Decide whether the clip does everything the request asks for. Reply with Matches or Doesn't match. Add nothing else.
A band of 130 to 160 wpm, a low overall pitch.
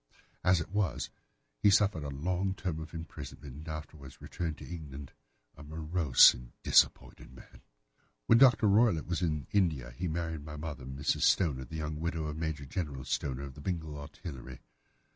Doesn't match